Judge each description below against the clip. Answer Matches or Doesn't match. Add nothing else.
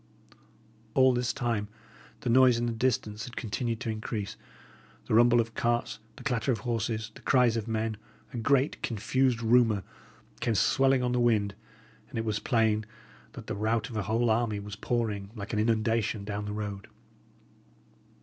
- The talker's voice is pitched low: Matches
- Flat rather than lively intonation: Matches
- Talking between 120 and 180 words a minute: Matches